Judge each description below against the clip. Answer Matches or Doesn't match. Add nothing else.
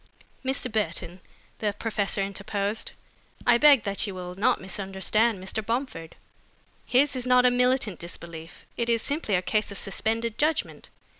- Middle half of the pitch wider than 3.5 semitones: Matches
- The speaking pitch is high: Matches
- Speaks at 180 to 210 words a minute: Doesn't match